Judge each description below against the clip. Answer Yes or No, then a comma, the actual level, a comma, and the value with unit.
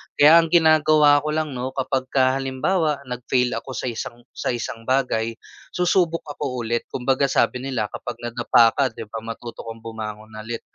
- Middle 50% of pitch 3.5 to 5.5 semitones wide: Yes, average, 3.8 semitones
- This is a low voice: Yes, low, 130 Hz